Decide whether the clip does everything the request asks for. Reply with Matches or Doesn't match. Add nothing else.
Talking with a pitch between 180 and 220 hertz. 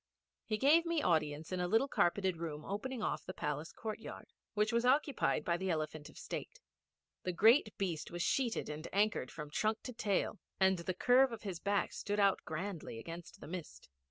Matches